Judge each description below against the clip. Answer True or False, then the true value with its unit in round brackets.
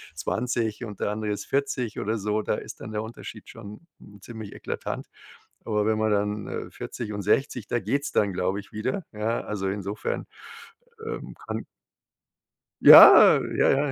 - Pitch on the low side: True (110 Hz)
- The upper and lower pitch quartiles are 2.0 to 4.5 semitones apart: True (2.4 semitones)